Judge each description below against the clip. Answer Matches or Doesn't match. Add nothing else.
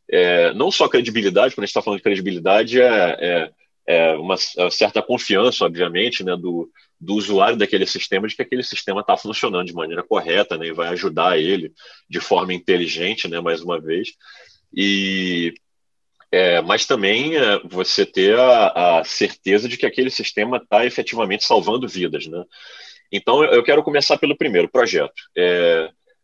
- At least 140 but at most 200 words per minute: Matches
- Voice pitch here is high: Doesn't match